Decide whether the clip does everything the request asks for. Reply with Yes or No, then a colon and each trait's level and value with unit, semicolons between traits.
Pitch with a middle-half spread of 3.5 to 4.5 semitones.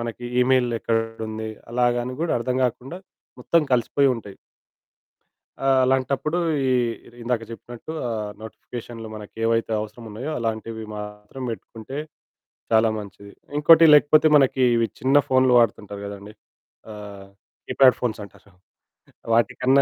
No: average, 3.1 semitones